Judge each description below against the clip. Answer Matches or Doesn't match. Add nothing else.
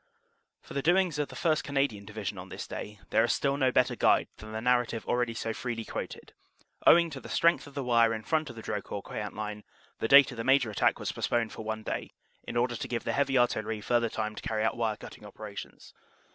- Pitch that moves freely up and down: Doesn't match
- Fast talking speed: Matches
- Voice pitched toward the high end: Doesn't match